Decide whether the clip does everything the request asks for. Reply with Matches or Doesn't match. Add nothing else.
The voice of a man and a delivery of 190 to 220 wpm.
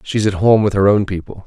Doesn't match